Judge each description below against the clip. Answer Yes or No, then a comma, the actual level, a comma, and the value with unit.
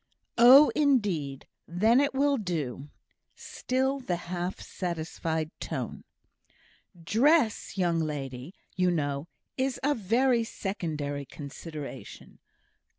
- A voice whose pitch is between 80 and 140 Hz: No, medium, 180 Hz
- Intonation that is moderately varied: No, wide, 8.5 semitones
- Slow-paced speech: Yes, slow, 95 wpm